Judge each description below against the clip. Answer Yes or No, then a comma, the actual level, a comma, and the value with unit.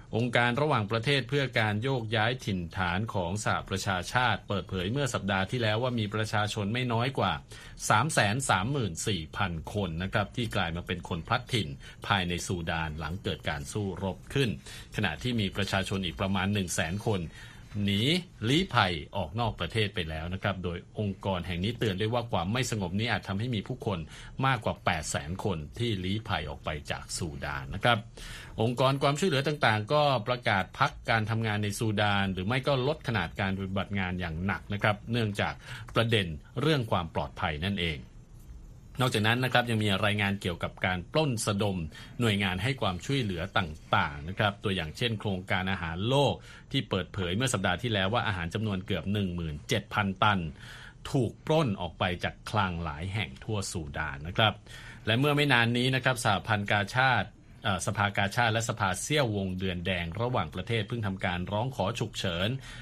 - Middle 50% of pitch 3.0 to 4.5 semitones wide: Yes, average, 4.1 semitones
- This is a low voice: Yes, low, 105 Hz